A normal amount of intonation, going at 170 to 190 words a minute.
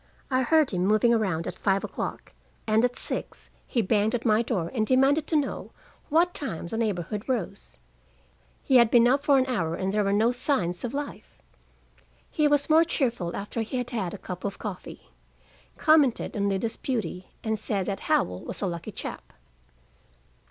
Yes: average, 5.0 semitones; average, 185 wpm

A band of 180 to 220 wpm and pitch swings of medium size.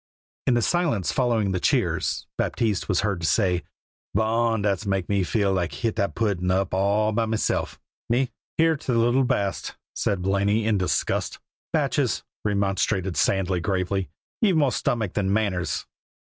No: average, 155 wpm; average, 3.0 semitones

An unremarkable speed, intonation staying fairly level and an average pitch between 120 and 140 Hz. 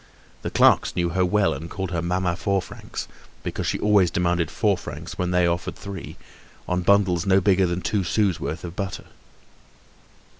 No: average, 180 wpm; narrow, 2.0 semitones; very low, 90 Hz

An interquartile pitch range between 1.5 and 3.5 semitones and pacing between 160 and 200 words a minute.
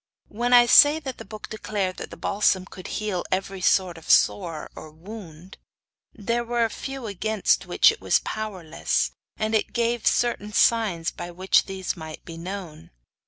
No: average, 4.2 semitones; average, 170 wpm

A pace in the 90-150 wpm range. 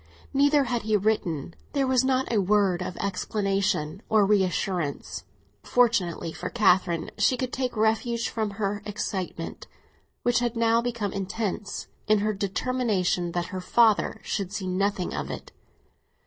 Yes: average, 145 wpm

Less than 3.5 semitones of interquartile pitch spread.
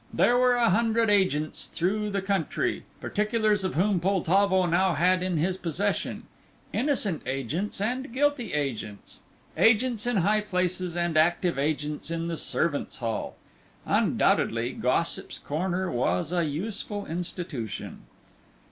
No: average, 4.7 semitones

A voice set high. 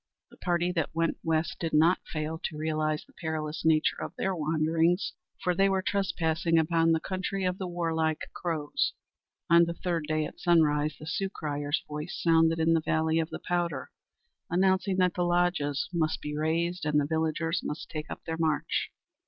No: medium, 165 Hz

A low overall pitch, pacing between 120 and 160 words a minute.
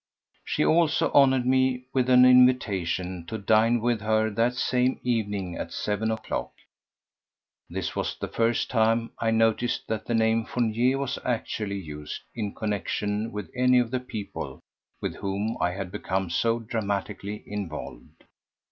Yes: low, 110 Hz; average, 155 wpm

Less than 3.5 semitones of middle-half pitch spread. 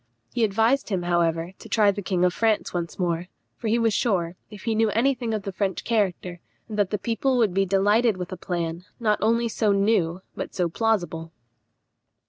No: average, 4.0 semitones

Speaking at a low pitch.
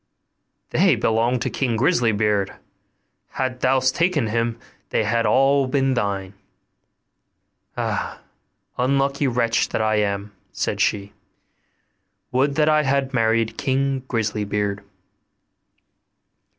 Yes: low, 120 Hz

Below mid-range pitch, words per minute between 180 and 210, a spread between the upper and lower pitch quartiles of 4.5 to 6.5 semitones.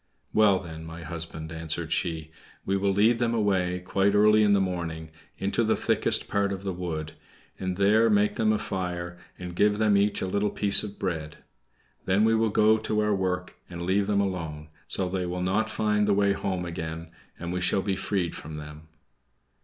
No: very low, 95 Hz; average, 200 wpm; average, 3.1 semitones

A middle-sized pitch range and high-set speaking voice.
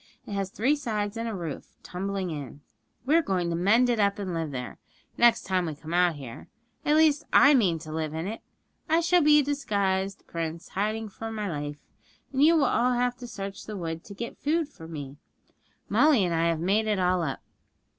No: wide, 6.4 semitones; high, 200 Hz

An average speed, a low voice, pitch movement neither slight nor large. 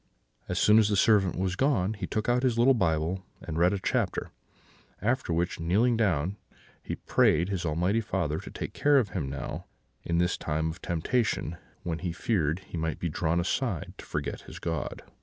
Yes: average, 190 wpm; very low, 90 Hz; average, 4.7 semitones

